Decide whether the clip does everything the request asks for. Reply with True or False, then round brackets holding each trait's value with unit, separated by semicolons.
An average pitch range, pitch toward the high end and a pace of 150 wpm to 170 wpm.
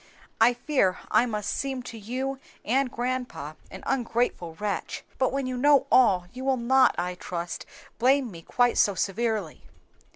True (4.7 semitones; 240 Hz; 160 wpm)